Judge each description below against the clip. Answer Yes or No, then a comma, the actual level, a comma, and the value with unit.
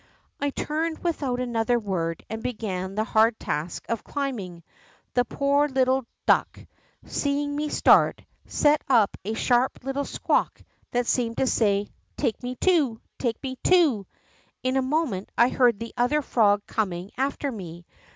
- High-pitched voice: Yes, high, 245 Hz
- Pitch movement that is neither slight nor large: Yes, average, 4.8 semitones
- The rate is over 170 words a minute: No, average, 160 wpm